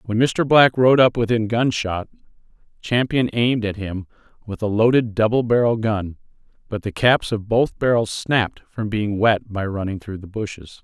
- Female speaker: No, male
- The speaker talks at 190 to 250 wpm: No, average, 175 wpm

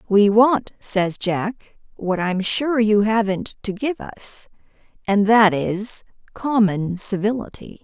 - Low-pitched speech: No, high, 210 Hz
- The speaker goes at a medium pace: No, slow, 125 wpm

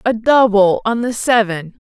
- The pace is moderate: Yes, average, 160 wpm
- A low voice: No, high, 220 Hz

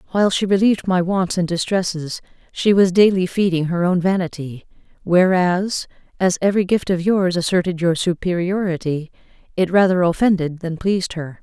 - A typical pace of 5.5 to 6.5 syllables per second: No, 5.3 syllables/s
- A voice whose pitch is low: No, medium, 180 Hz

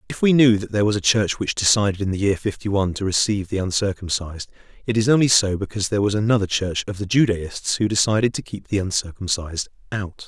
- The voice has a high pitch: No, low, 100 Hz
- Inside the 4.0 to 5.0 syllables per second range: No, 6.6 syllables/s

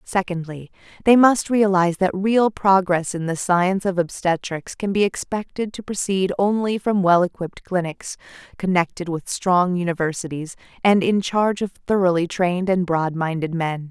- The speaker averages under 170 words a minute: Yes, average, 155 wpm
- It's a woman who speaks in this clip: Yes, female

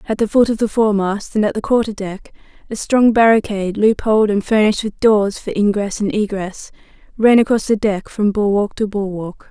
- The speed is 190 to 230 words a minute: Yes, average, 200 wpm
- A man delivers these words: No, female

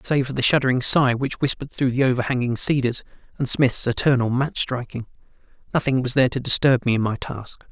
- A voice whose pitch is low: Yes, low, 125 Hz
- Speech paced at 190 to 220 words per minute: Yes, average, 200 wpm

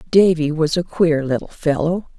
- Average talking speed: Yes, average, 165 wpm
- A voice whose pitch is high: No, medium, 165 Hz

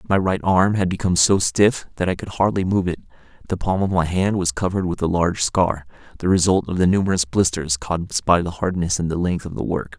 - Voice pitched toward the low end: Yes, very low, 90 Hz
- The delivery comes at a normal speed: No, fast, 240 wpm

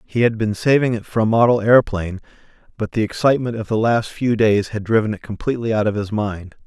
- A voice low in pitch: Yes, low, 110 Hz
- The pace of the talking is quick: Yes, fast, 225 wpm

